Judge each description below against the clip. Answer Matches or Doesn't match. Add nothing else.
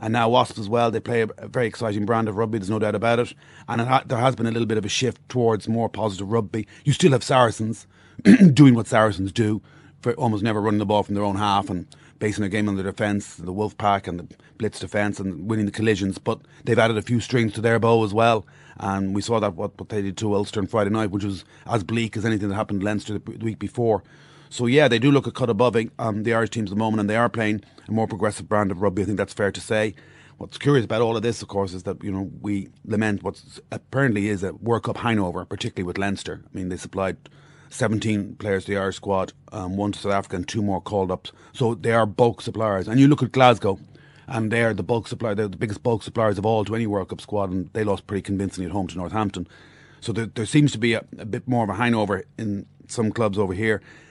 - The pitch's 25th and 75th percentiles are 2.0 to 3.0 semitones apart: Matches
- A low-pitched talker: Matches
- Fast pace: Matches